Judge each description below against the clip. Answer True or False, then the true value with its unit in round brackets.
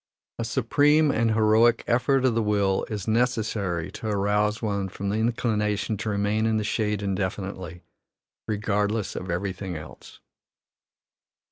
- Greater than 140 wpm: False (135 wpm)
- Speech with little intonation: True (2.3 semitones)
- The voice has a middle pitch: False (105 Hz)